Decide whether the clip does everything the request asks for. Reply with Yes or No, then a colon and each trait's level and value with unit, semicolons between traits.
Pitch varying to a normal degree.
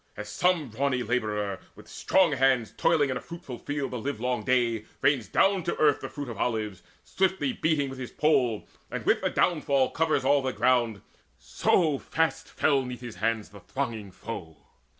Yes: average, 4.2 semitones